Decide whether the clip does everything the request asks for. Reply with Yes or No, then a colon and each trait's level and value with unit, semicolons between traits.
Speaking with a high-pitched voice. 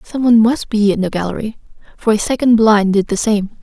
Yes: high, 215 Hz